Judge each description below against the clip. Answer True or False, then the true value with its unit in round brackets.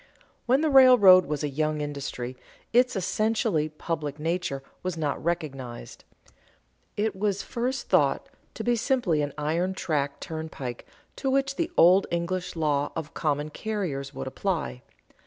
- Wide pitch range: True (6.1 semitones)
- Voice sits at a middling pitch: True (165 Hz)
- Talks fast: False (150 wpm)